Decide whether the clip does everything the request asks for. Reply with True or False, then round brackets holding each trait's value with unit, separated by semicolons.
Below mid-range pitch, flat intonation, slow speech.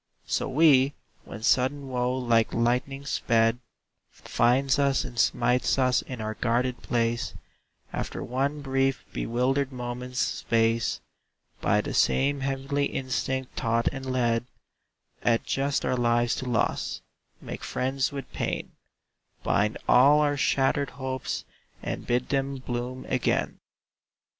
True (130 Hz; 2.1 semitones; 125 wpm)